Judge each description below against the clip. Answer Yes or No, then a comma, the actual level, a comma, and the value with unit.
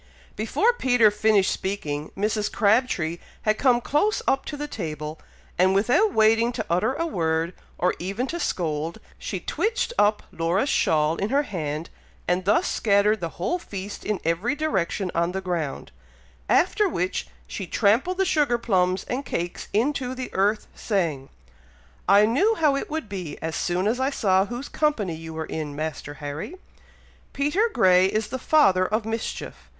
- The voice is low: No, high, 205 Hz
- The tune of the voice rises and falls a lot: Yes, wide, 6.9 semitones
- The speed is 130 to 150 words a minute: No, average, 165 wpm